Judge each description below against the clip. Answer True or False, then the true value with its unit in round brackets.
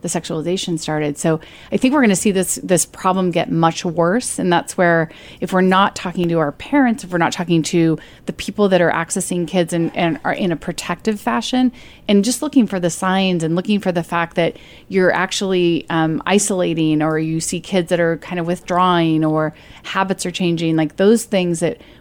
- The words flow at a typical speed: False (210 wpm)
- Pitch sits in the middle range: True (175 Hz)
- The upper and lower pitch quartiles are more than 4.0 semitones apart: False (2.5 semitones)